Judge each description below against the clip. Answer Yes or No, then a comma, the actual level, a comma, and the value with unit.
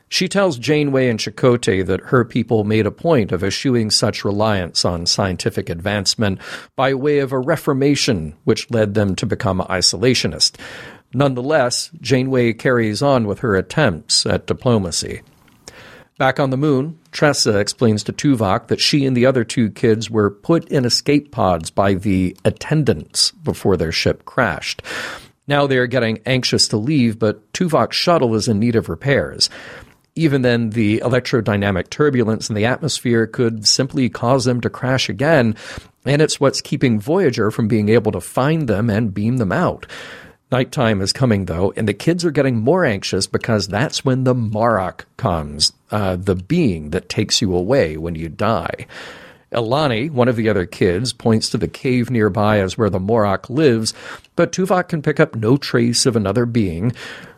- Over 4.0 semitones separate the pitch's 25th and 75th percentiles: Yes, average, 4.4 semitones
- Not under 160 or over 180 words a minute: Yes, average, 170 wpm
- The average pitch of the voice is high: No, low, 115 Hz